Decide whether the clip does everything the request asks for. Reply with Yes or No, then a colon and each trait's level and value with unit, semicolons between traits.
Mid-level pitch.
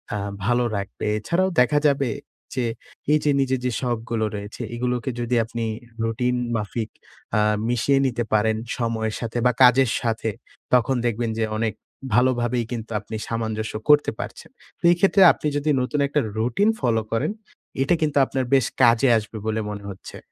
No: low, 120 Hz